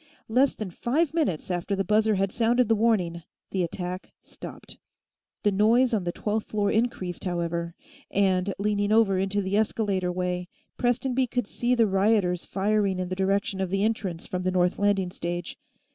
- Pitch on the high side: Yes, high, 200 Hz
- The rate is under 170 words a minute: No, average, 175 wpm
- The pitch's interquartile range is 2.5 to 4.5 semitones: Yes, average, 3.3 semitones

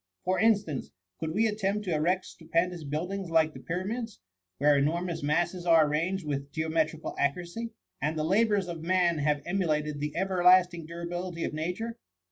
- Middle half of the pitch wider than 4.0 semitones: No, average, 3.2 semitones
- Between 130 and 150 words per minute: No, average, 160 wpm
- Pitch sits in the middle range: Yes, medium, 170 Hz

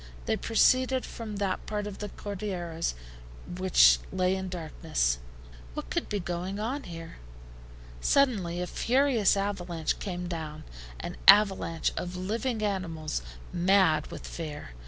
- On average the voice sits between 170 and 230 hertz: Yes, medium, 185 Hz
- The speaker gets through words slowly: Yes, slow, 130 wpm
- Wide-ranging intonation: No, average, 3.6 semitones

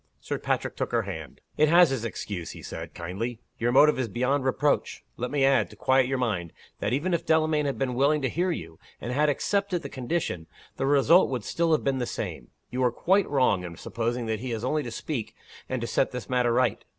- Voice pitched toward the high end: No, low, 130 Hz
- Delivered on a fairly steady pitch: No, average, 4.2 semitones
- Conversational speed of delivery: No, fast, 230 wpm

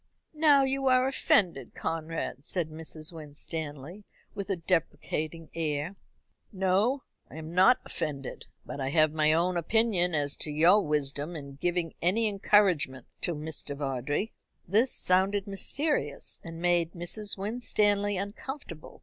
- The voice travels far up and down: No, average, 4.8 semitones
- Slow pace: Yes, slow, 130 wpm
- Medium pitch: Yes, medium, 170 Hz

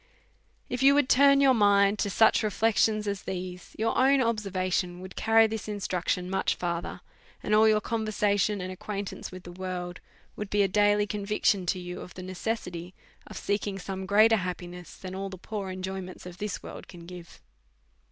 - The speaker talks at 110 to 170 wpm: No, average, 185 wpm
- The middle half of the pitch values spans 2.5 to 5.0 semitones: Yes, average, 2.8 semitones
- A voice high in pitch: Yes, high, 200 Hz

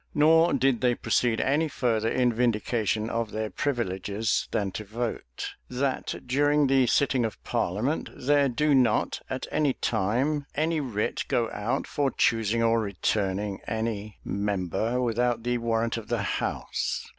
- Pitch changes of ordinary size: Yes, average, 3.6 semitones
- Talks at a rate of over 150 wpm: No, average, 145 wpm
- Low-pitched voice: Yes, low, 115 Hz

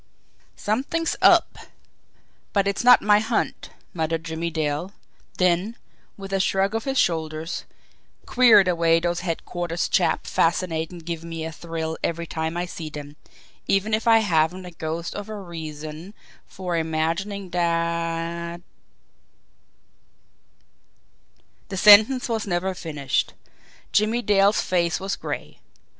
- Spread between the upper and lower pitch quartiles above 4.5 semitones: No, average, 3.4 semitones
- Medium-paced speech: No, slow, 130 wpm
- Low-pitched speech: No, medium, 175 Hz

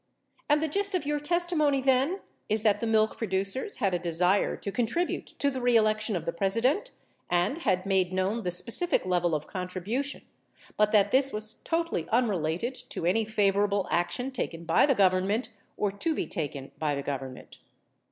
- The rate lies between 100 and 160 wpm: No, average, 180 wpm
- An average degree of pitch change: No, wide, 6.4 semitones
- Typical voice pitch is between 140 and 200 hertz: No, high, 210 Hz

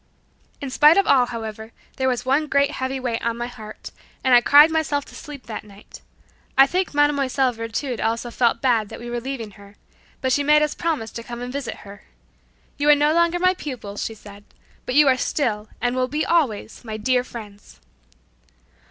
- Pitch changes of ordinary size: Yes, average, 4.2 semitones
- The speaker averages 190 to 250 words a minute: Yes, average, 200 wpm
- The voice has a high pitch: Yes, very high, 255 Hz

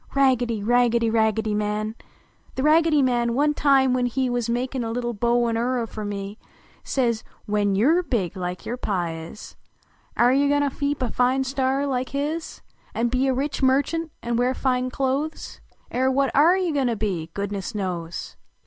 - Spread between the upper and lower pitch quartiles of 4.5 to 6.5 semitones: No, average, 3.7 semitones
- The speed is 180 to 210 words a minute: Yes, average, 190 wpm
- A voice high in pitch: Yes, high, 245 Hz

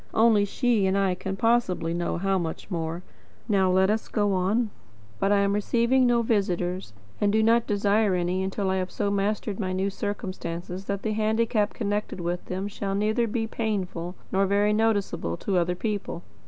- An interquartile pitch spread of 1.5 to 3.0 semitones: Yes, narrow, 2.6 semitones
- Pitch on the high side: Yes, high, 200 Hz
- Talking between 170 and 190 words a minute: Yes, average, 180 wpm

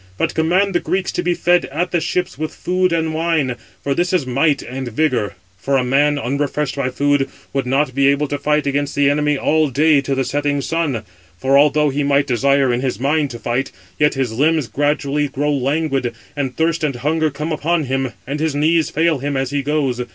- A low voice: No, medium, 145 Hz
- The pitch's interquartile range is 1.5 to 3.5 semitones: Yes, narrow, 2.6 semitones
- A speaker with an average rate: No, fast, 215 wpm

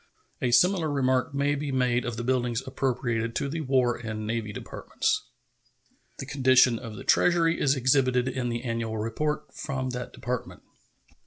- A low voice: Yes, low, 130 Hz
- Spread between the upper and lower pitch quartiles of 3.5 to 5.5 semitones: No, average, 2.7 semitones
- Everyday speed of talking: Yes, average, 160 wpm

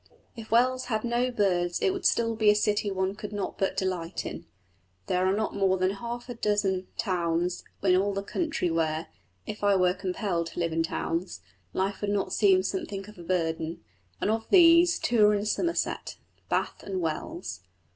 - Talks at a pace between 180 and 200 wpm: Yes, average, 190 wpm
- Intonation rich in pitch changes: No, average, 3.2 semitones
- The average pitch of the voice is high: Yes, high, 195 Hz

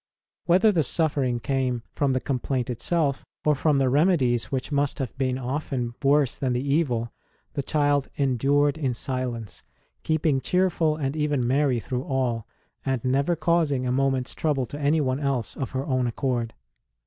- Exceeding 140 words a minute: Yes, average, 165 wpm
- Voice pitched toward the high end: No, low, 135 Hz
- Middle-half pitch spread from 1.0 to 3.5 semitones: Yes, narrow, 2.6 semitones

